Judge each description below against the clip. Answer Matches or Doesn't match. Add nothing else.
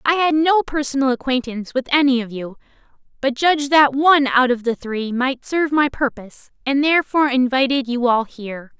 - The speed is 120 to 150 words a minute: Doesn't match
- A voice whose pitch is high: Matches